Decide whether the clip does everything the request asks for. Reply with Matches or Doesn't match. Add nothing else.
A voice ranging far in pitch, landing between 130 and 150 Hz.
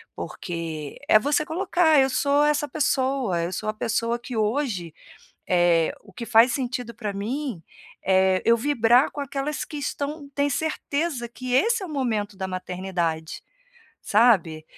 Doesn't match